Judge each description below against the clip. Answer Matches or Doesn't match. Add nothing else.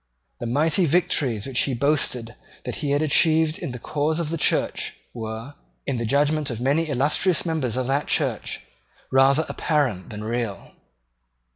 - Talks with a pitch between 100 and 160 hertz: Matches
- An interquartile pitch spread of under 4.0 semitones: Doesn't match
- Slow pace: Doesn't match